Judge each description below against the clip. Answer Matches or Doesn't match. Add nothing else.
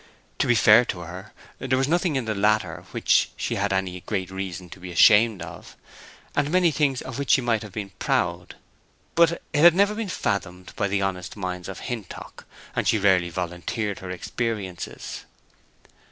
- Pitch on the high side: Doesn't match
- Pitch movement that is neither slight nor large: Doesn't match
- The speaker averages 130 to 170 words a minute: Doesn't match